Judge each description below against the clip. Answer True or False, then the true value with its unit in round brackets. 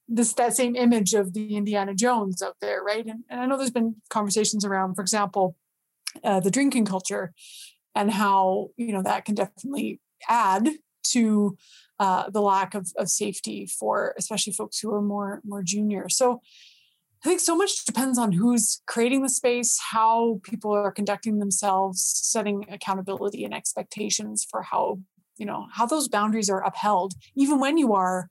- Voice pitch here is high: True (210 Hz)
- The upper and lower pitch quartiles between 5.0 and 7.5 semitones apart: False (3.3 semitones)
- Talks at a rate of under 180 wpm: True (170 wpm)